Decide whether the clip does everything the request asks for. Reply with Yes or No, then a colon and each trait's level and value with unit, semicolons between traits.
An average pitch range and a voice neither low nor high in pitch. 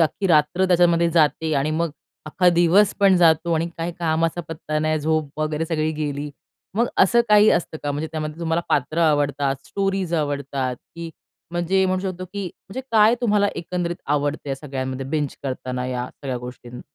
Yes: average, 3.3 semitones; medium, 160 Hz